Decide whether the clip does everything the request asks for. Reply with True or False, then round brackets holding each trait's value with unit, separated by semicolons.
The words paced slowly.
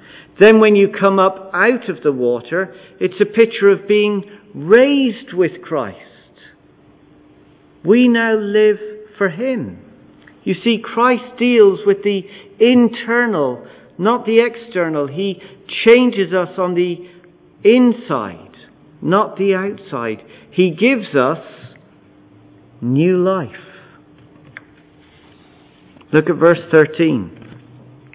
True (105 wpm)